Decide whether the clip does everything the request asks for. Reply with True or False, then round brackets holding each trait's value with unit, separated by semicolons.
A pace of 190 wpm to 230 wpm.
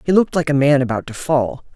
False (275 wpm)